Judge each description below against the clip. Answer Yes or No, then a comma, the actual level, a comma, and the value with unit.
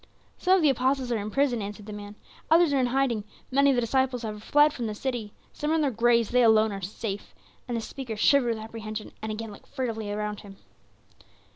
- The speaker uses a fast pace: Yes, fast, 230 wpm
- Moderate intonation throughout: Yes, average, 3.9 semitones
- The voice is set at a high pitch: Yes, high, 230 Hz